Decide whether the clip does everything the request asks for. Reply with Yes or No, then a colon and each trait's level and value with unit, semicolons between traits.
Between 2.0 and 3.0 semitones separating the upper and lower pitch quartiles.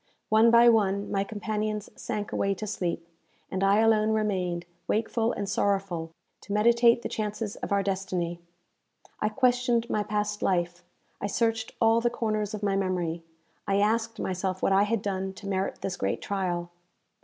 Yes: narrow, 2.6 semitones